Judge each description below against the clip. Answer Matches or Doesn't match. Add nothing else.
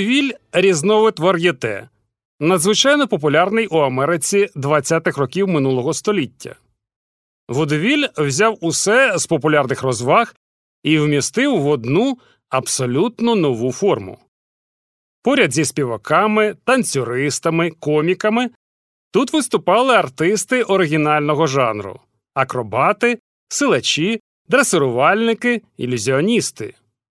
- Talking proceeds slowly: Matches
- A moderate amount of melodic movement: Doesn't match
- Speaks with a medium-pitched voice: Matches